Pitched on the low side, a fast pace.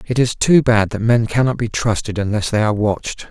Yes: low, 110 Hz; fast, 235 wpm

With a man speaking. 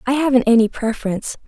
No: female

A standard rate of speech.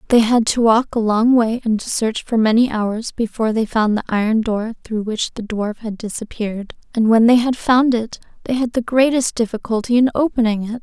No: fast, 215 wpm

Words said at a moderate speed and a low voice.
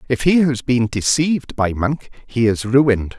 Yes: average, 190 wpm; low, 125 Hz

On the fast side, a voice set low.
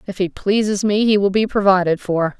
No: fast, 225 wpm; high, 195 Hz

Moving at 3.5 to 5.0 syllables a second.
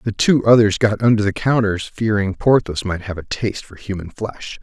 No: 5.2 syllables/s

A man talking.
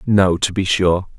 Yes: male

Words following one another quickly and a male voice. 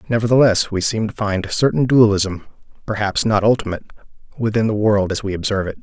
No: average, 185 wpm; male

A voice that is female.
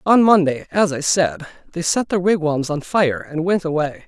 No: male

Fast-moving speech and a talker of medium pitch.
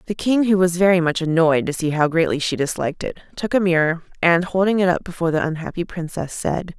Yes: fast, 230 wpm; medium, 175 Hz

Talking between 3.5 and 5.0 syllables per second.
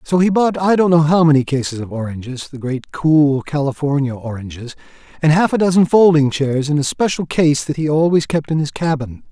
No: 5.4 syllables/s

